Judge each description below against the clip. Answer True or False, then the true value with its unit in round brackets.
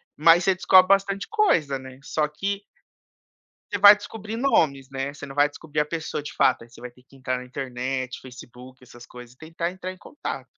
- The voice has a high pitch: False (145 Hz)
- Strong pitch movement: True (6.3 semitones)